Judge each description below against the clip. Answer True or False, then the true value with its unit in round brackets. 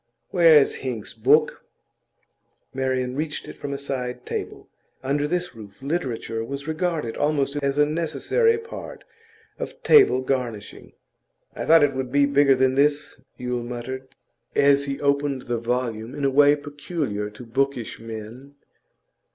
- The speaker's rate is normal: True (145 wpm)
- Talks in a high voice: False (140 Hz)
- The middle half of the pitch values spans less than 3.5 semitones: True (2.9 semitones)